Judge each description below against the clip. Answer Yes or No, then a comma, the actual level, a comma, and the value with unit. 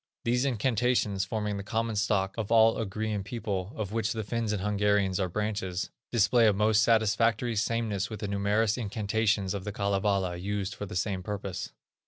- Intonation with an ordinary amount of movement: No, narrow, 2.1 semitones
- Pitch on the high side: No, low, 105 Hz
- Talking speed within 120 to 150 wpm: No, average, 175 wpm